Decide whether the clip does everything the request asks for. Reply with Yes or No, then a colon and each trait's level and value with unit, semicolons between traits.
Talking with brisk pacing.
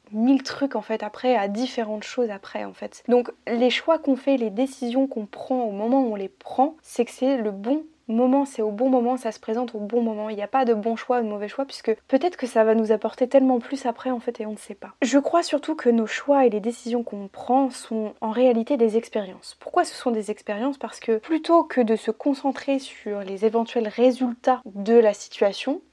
Yes: fast, 245 wpm